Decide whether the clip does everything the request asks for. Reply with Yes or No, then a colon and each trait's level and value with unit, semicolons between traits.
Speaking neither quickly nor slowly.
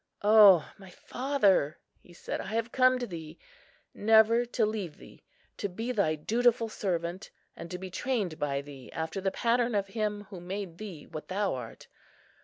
Yes: average, 170 wpm